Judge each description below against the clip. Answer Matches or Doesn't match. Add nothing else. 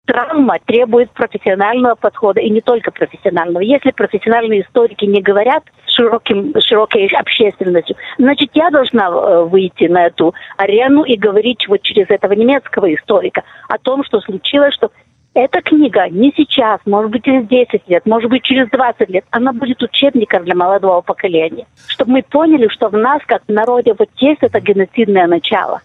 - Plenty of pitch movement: Doesn't match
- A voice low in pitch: Doesn't match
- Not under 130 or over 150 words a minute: Doesn't match